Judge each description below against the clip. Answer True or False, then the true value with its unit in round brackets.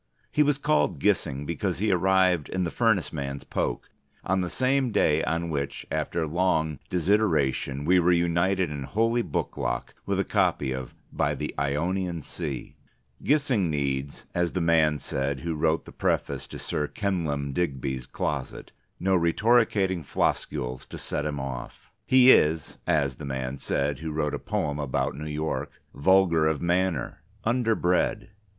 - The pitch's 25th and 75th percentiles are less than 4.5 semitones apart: False (4.8 semitones)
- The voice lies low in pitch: True (80 Hz)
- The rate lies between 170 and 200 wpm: False (155 wpm)